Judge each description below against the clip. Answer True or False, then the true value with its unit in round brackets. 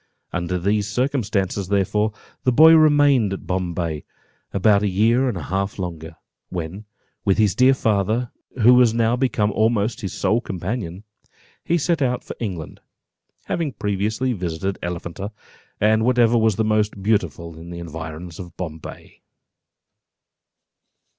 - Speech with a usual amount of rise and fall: True (4.7 semitones)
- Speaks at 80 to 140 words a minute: True (135 wpm)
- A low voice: True (105 Hz)